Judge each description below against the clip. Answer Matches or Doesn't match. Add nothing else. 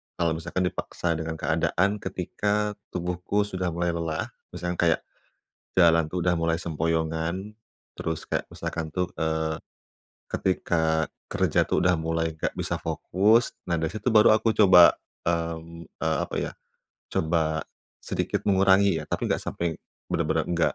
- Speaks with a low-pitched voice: Matches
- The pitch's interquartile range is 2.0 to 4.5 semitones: Matches